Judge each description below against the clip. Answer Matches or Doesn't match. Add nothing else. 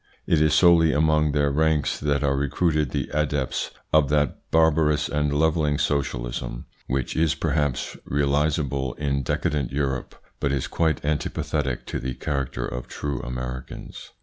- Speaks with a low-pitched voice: Matches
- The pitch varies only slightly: Matches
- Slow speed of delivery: Doesn't match